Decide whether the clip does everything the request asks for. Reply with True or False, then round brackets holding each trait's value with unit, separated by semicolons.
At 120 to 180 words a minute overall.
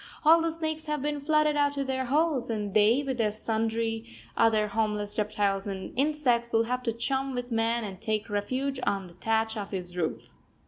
False (190 wpm)